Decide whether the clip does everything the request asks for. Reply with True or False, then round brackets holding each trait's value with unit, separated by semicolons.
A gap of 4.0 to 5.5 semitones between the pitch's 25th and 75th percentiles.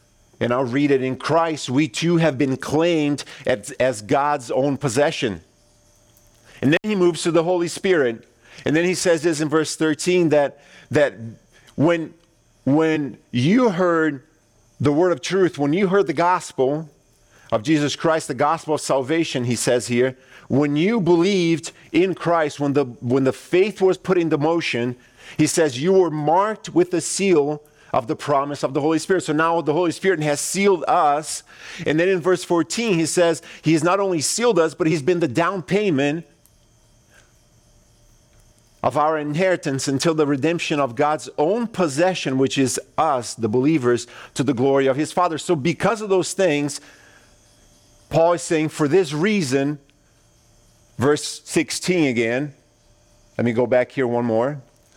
True (4.7 semitones)